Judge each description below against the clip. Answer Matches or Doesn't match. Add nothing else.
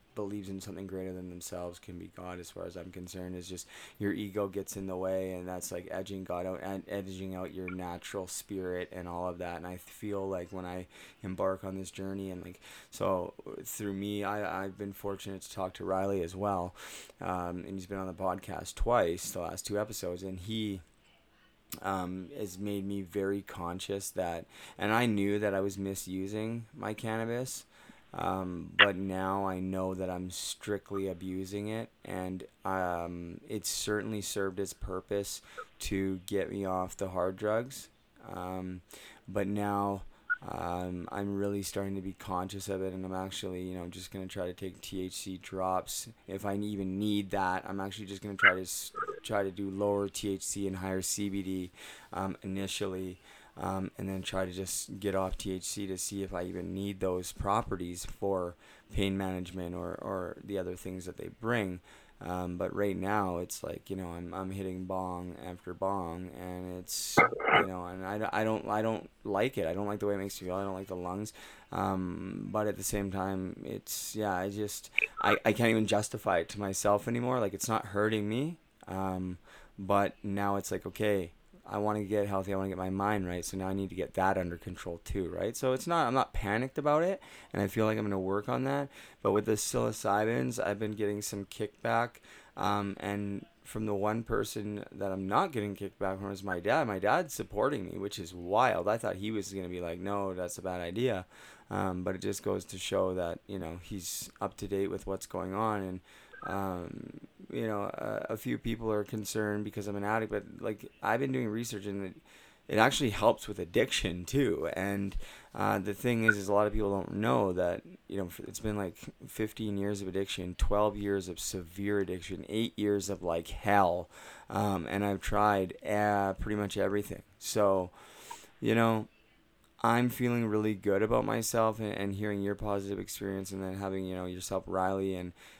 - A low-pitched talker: Matches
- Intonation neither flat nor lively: Doesn't match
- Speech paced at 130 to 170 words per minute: Doesn't match